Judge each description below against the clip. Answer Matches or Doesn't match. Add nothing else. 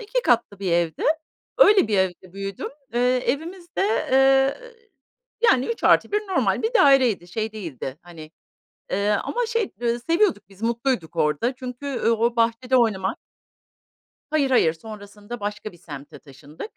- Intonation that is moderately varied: Doesn't match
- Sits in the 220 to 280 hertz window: Matches